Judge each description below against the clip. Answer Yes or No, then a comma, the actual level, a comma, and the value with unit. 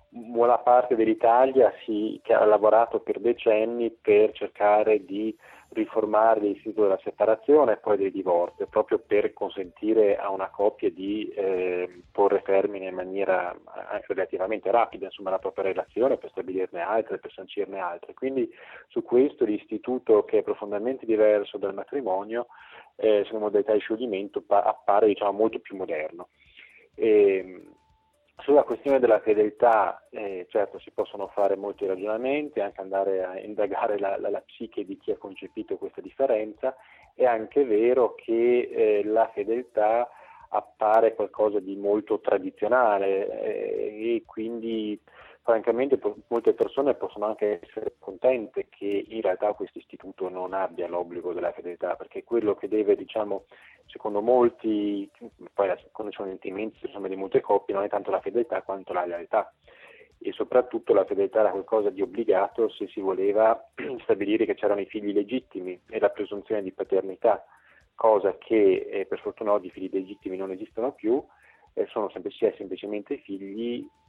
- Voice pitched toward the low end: Yes, low, 120 Hz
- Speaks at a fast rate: No, average, 150 wpm